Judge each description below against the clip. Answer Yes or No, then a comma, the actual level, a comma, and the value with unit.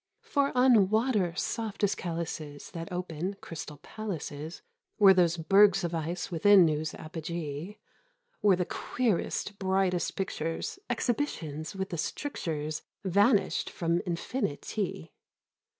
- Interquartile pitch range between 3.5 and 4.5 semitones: Yes, average, 4.0 semitones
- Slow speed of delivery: Yes, slow, 120 wpm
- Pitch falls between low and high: Yes, medium, 180 Hz